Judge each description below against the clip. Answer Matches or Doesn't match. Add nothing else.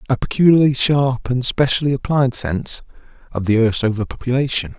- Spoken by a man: Matches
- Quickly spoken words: Doesn't match